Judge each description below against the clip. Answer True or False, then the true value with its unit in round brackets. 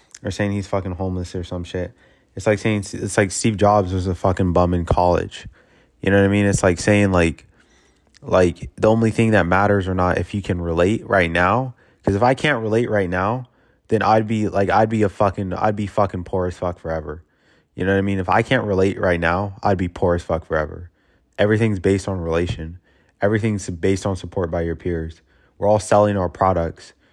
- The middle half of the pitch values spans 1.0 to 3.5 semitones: True (2.7 semitones)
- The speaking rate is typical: False (220 wpm)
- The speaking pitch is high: False (95 Hz)